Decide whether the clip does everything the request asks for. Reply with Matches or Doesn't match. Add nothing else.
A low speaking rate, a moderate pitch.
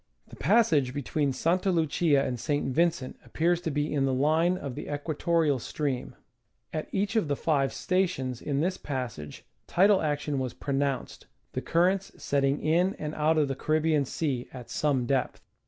Doesn't match